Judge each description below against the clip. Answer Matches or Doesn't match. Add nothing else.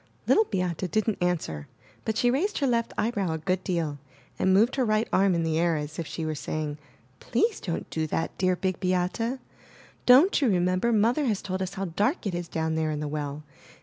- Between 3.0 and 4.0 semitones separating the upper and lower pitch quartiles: Doesn't match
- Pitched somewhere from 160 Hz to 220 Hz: Matches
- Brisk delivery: Matches